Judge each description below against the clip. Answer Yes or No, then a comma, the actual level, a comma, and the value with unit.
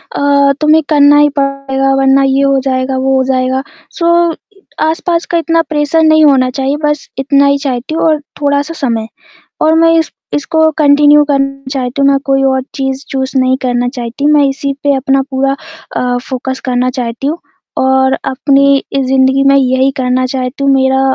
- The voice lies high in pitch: Yes, very high, 275 Hz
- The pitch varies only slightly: Yes, narrow, 1.7 semitones